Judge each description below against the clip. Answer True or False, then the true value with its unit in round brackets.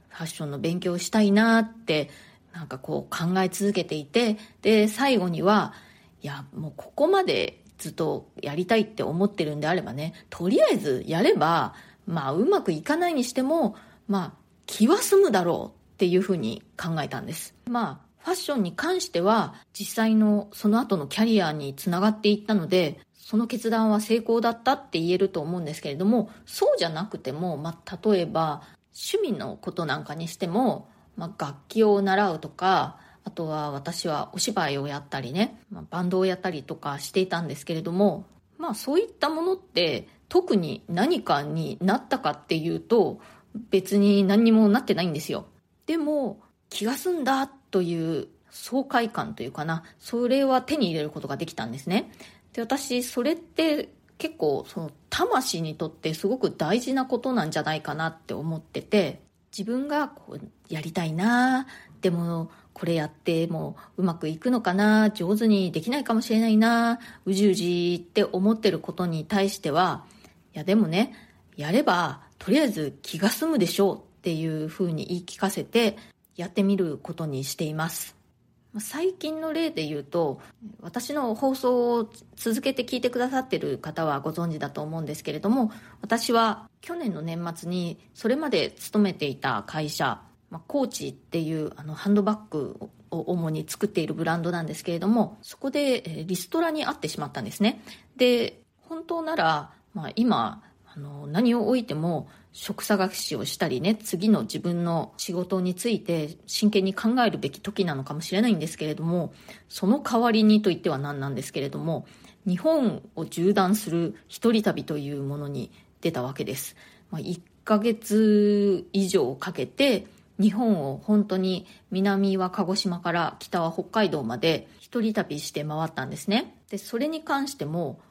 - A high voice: True (195 Hz)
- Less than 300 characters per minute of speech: False (330 characters per minute)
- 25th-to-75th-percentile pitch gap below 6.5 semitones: True (5.6 semitones)